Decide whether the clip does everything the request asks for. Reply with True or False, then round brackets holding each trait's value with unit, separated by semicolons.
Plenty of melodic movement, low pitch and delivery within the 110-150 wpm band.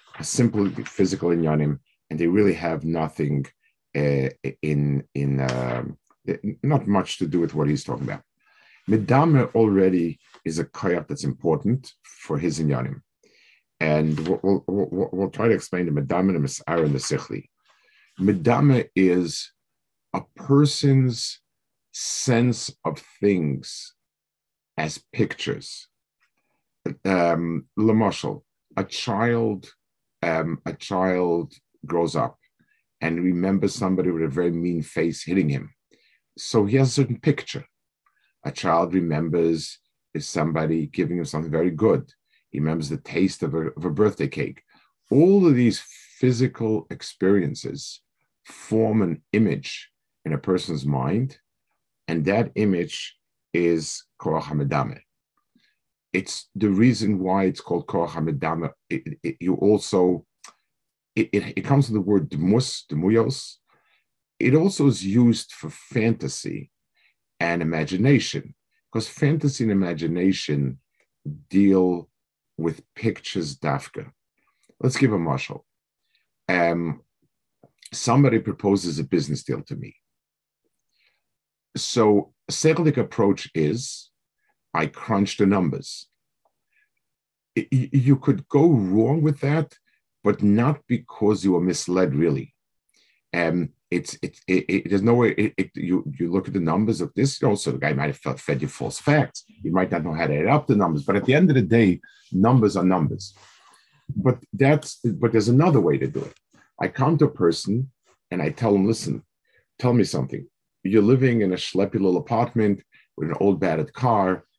True (6.1 semitones; 100 Hz; 140 wpm)